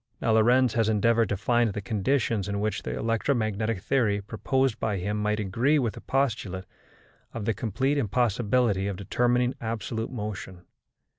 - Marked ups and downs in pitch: No, average, 3.1 semitones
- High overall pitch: No, low, 110 Hz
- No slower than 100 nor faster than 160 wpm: Yes, average, 155 wpm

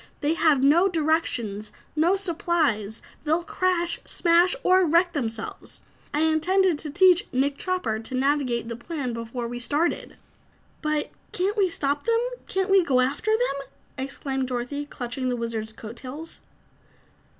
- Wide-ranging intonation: Yes, wide, 5.7 semitones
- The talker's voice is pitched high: Yes, very high, 295 Hz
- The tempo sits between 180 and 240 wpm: No, average, 145 wpm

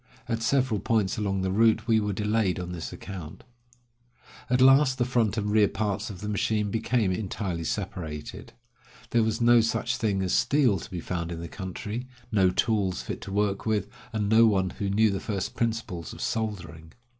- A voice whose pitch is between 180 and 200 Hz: No, low, 105 Hz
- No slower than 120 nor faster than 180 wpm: No, average, 190 wpm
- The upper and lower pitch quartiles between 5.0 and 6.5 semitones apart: No, average, 3.1 semitones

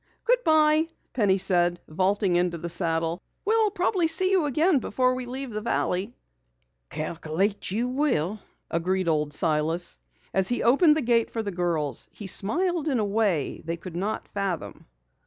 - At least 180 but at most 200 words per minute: No, average, 155 wpm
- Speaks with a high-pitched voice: Yes, high, 205 Hz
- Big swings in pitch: Yes, wide, 8.1 semitones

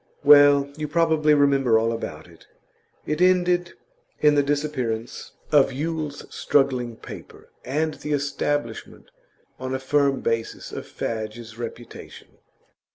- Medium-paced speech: No, slow, 120 wpm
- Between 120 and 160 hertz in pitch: Yes, medium, 140 Hz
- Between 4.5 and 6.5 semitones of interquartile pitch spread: No, average, 3.7 semitones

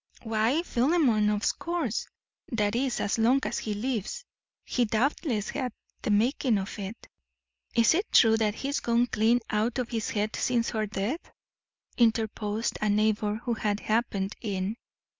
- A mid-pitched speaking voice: No, high, 225 Hz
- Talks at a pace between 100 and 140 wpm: No, average, 155 wpm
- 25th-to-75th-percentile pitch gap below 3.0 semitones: Yes, narrow, 2.6 semitones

